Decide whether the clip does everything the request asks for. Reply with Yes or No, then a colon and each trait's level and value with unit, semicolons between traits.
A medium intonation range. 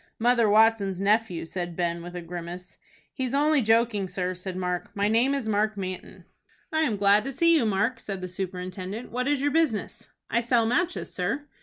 Yes: average, 5.0 semitones